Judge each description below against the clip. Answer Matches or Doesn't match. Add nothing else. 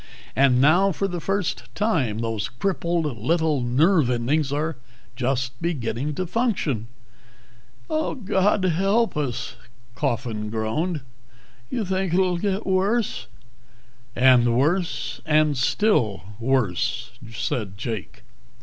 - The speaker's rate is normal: Doesn't match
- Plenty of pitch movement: Matches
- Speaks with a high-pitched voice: Doesn't match